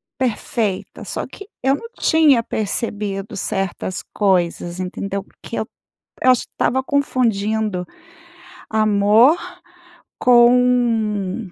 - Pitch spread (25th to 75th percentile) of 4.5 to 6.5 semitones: No, average, 4.1 semitones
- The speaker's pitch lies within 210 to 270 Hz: Yes, high, 215 Hz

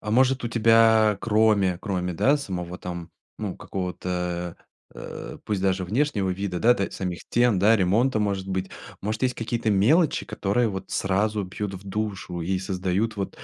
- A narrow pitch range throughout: No, average, 3.3 semitones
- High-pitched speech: No, low, 100 Hz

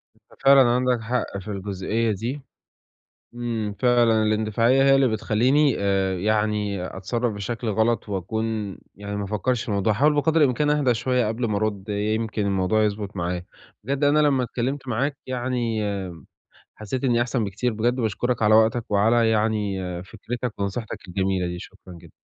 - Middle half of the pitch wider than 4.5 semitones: No, average, 3.3 semitones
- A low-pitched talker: Yes, low, 110 Hz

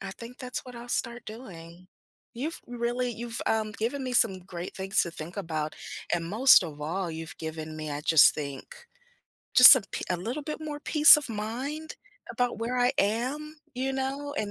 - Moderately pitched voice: No, high, 230 Hz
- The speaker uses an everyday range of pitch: No, wide, 6.9 semitones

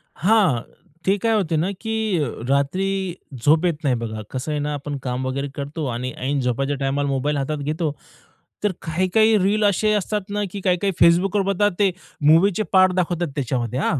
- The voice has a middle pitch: Yes, medium, 160 Hz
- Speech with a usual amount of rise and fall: No, wide, 5.9 semitones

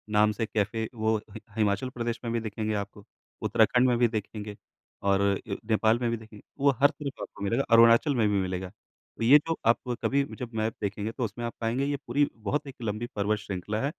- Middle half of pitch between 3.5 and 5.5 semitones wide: No, narrow, 2.6 semitones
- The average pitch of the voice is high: No, low, 110 Hz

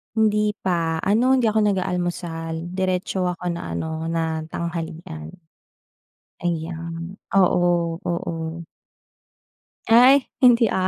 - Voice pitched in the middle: Yes, medium, 175 Hz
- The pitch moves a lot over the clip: No, average, 3.1 semitones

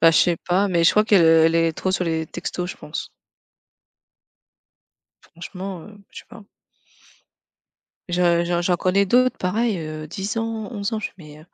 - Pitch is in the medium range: Yes, medium, 180 Hz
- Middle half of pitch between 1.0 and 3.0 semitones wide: No, average, 3.5 semitones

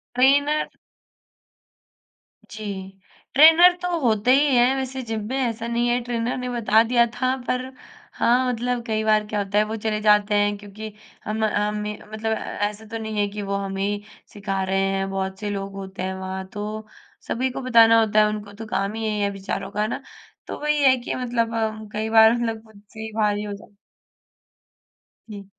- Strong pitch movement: No, average, 2.8 semitones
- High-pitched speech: Yes, high, 220 Hz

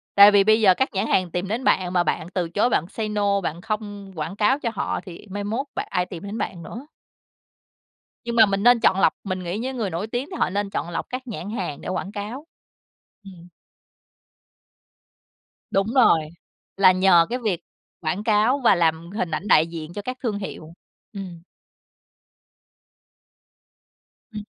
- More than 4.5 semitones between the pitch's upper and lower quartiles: No, average, 3.6 semitones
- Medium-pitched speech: No, high, 200 Hz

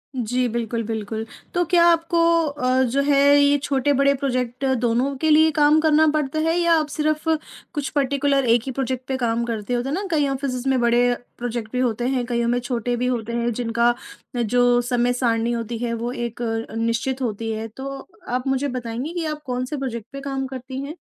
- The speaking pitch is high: Yes, very high, 255 Hz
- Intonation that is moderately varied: Yes, average, 3.0 semitones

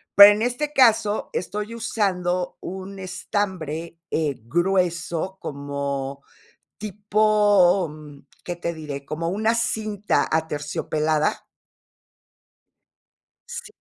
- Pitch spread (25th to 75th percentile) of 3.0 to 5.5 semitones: Yes, average, 4.9 semitones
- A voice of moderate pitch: Yes, medium, 180 Hz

